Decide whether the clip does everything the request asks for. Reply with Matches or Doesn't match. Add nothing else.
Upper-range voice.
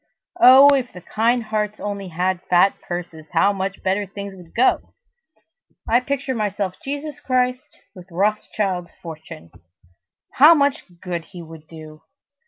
Matches